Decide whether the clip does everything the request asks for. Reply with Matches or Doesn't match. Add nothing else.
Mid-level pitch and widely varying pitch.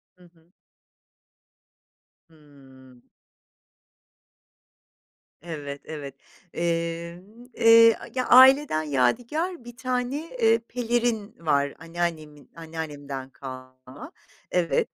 Matches